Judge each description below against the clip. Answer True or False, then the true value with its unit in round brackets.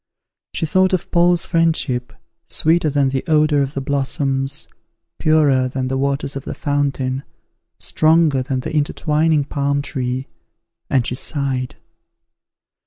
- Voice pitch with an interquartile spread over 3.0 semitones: False (2.7 semitones)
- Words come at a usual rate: False (130 wpm)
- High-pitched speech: False (140 Hz)